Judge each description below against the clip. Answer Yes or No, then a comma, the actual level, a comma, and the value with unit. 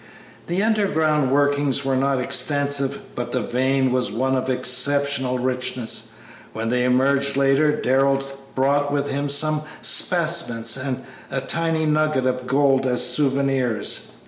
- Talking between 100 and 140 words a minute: Yes, slow, 135 wpm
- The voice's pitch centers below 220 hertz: Yes, low, 135 Hz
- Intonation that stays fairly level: Yes, narrow, 2.1 semitones